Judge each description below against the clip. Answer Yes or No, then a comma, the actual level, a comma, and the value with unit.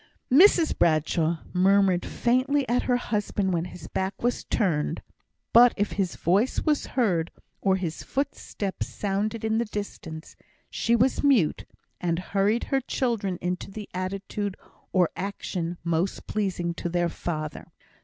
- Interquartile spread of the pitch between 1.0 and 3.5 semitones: No, average, 4.7 semitones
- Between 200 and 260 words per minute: No, average, 140 wpm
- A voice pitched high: Yes, high, 195 Hz